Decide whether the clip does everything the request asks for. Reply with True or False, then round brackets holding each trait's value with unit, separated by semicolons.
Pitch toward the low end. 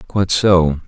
True (90 Hz)